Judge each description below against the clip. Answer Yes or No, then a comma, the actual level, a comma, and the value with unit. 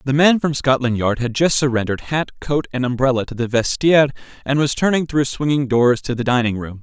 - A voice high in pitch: No, low, 130 Hz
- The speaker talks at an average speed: No, fast, 220 wpm